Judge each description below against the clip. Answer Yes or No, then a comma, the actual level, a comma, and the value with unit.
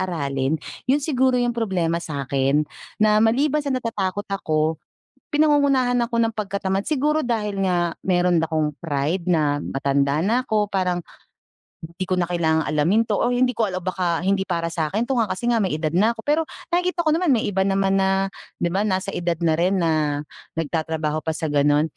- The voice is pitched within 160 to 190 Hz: Yes, medium, 185 Hz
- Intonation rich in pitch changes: Yes, wide, 6.1 semitones